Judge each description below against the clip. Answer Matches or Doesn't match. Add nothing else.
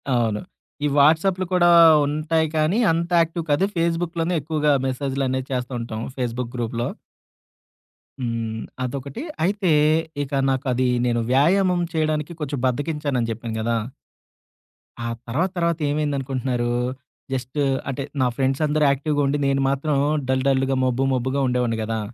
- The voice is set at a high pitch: Doesn't match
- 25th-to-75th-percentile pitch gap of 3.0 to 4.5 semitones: Matches